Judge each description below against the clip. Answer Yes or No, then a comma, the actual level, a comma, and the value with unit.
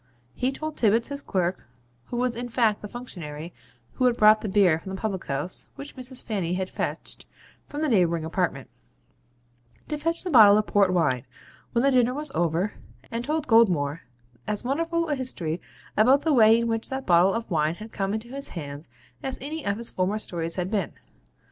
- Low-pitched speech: No, high, 215 Hz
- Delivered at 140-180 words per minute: No, average, 195 wpm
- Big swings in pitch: Yes, wide, 6.1 semitones